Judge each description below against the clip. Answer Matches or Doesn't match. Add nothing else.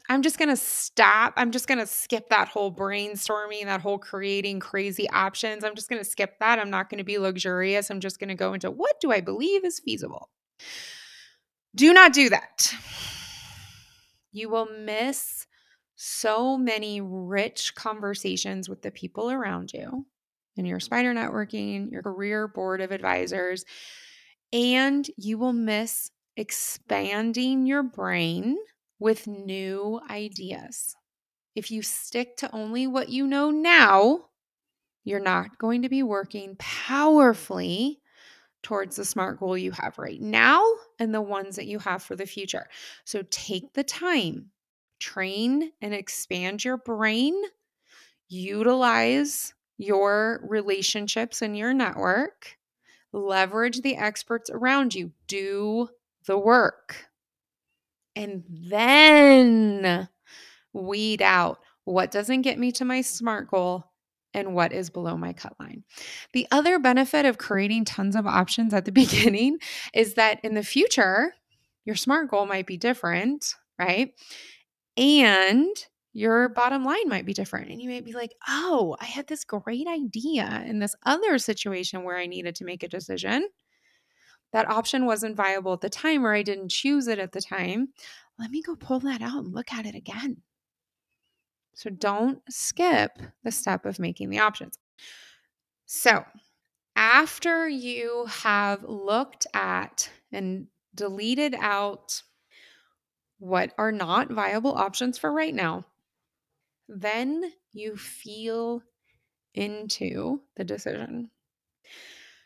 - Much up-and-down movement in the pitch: Doesn't match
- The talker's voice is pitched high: Matches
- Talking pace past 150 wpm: Doesn't match